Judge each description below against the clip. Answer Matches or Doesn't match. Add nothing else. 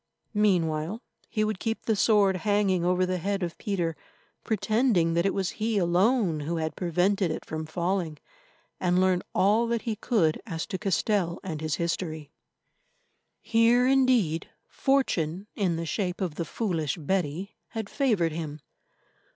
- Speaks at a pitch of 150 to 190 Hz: Matches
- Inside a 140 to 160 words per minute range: Matches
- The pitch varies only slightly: Doesn't match